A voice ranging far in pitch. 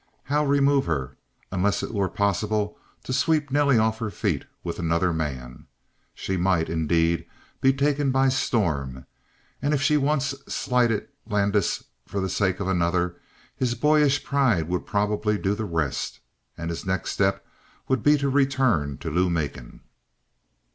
Yes: wide, 7.8 semitones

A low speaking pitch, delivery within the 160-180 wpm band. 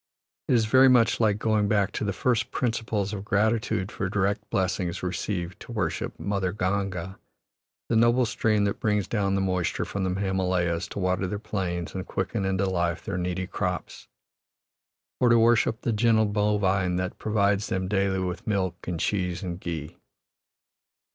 Yes: low, 100 Hz; average, 165 wpm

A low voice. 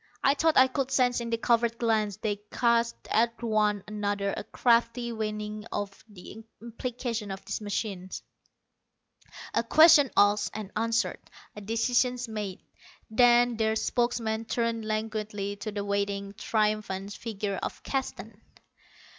No: high, 220 Hz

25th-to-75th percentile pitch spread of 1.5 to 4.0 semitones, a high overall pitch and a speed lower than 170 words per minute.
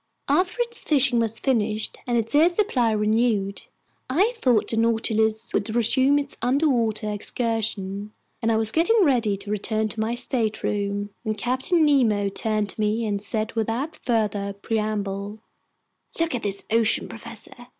Yes: average, 2.9 semitones; high, 225 Hz; average, 150 wpm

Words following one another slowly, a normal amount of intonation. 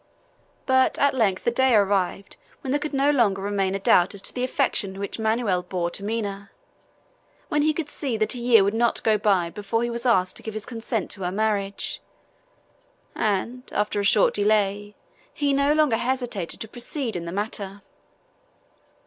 No: average, 185 wpm; average, 3.9 semitones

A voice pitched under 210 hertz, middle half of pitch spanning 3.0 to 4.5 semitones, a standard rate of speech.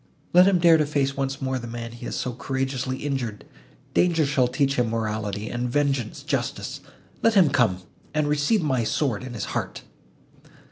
Yes: low, 135 Hz; average, 3.7 semitones; average, 175 wpm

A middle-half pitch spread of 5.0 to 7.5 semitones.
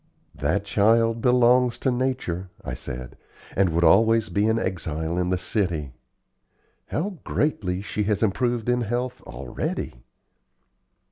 Yes: wide, 5.5 semitones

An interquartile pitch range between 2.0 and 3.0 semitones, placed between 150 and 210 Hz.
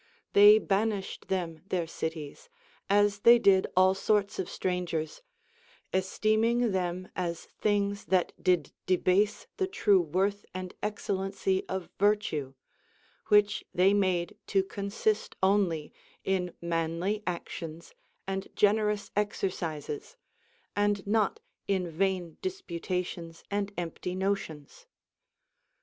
Yes: average, 2.7 semitones; high, 190 Hz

